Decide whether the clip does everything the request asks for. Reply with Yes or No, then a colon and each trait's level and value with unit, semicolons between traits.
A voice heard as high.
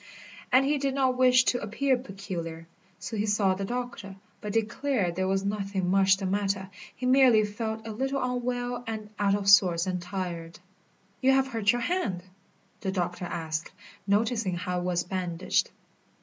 Yes: high, 205 Hz